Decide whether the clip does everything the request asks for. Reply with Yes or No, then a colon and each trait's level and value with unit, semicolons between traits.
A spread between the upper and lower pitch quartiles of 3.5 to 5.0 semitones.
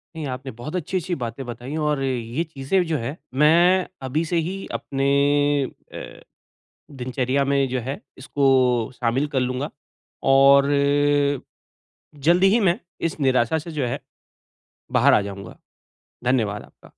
Yes: average, 4.0 semitones